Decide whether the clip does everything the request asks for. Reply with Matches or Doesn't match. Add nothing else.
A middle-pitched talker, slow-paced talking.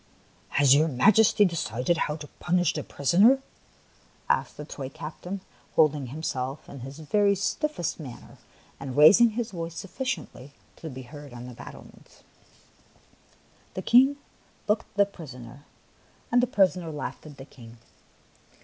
Doesn't match